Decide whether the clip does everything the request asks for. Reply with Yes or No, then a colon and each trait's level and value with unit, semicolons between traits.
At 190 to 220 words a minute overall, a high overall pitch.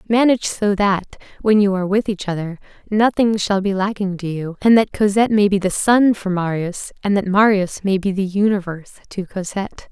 Yes: average, 200 wpm; high, 200 Hz